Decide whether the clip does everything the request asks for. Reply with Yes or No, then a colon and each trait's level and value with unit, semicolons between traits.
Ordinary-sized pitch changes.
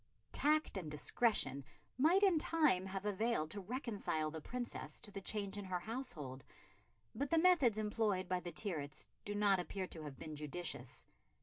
No: wide, 6.9 semitones